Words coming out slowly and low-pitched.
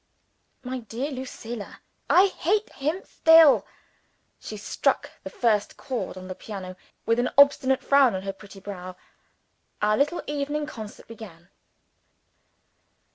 No: slow, 130 wpm; high, 240 Hz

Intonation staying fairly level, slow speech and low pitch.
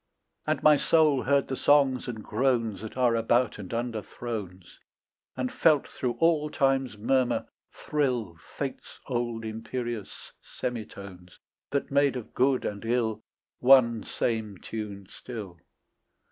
No: average, 3.4 semitones; slow, 130 wpm; low, 120 Hz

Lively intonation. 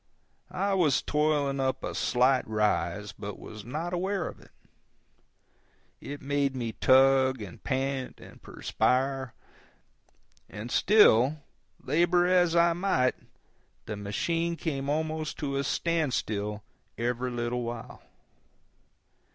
No: average, 4.9 semitones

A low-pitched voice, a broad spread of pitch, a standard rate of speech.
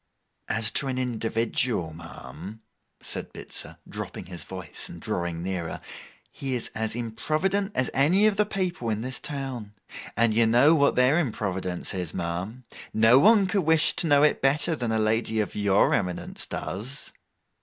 Yes: low, 115 Hz; wide, 5.9 semitones; average, 165 wpm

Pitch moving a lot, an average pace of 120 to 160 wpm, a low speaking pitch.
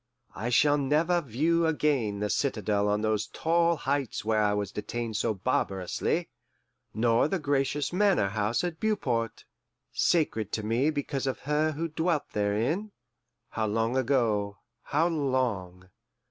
Yes: wide, 6.4 semitones; average, 140 wpm; low, 130 Hz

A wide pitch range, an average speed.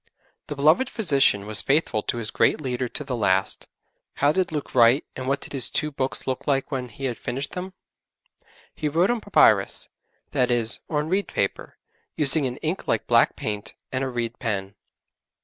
No: average, 4.1 semitones; average, 185 wpm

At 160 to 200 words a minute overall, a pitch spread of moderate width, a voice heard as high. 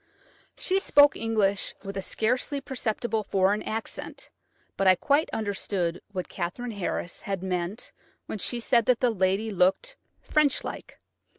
No: average, 140 wpm; average, 4.4 semitones; high, 215 Hz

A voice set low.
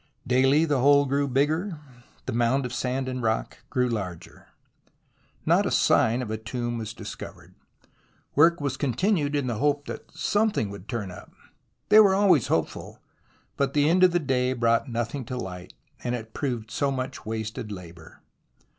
Yes: low, 130 Hz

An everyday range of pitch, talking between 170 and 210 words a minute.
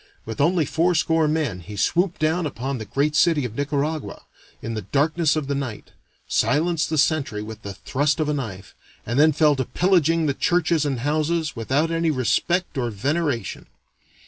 Yes: average, 4.1 semitones; average, 175 wpm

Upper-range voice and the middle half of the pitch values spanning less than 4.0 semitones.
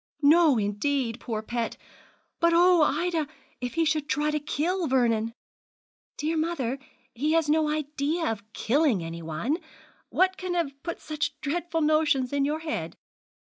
No: very high, 300 Hz; average, 4.6 semitones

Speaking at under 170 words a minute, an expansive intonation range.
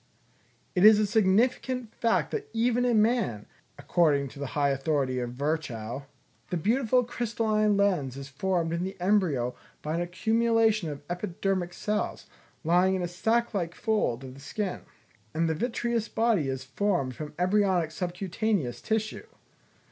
Yes: average, 150 wpm; wide, 6.7 semitones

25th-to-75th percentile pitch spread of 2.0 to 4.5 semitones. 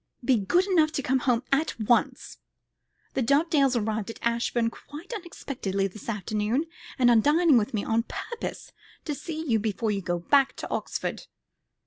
No: average, 5.3 semitones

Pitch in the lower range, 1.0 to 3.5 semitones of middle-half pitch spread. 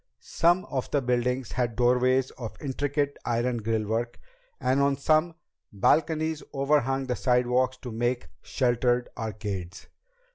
Yes: low, 125 Hz; narrow, 2.5 semitones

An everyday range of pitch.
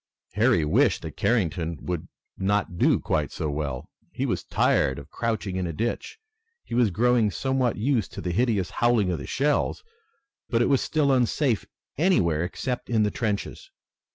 No: wide, 5.8 semitones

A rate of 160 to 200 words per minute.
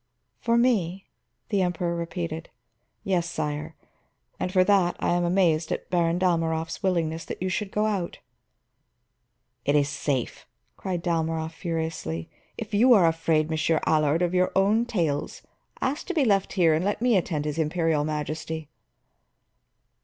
No: average, 150 wpm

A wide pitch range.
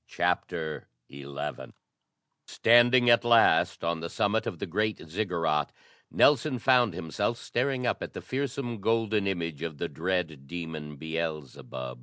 Yes: wide, 6.7 semitones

